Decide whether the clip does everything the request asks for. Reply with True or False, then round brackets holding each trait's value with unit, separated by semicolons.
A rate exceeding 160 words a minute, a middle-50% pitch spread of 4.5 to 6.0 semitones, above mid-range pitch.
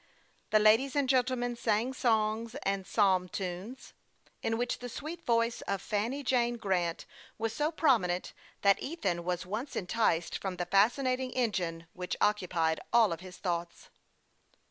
False (145 wpm; 5.2 semitones; 215 Hz)